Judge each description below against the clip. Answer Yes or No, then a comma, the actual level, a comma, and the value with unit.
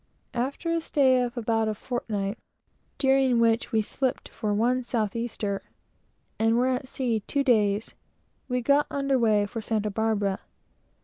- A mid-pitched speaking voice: No, high, 235 Hz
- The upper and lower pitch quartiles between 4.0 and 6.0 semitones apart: No, average, 3.1 semitones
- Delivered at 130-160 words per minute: Yes, average, 150 wpm